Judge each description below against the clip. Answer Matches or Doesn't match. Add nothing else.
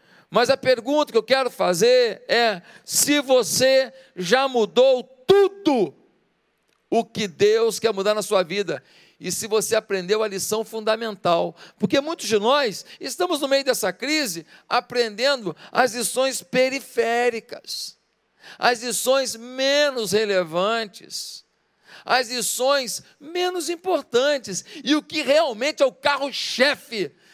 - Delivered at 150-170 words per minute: Doesn't match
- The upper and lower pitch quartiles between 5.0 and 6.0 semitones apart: Doesn't match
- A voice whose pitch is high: Matches